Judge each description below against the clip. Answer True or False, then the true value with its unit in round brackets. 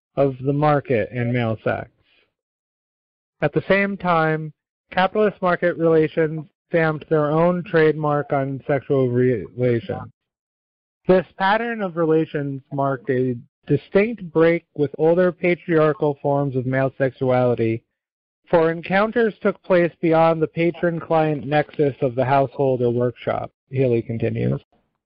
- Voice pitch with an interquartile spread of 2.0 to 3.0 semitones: False (4.1 semitones)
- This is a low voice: False (150 Hz)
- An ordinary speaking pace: False (120 wpm)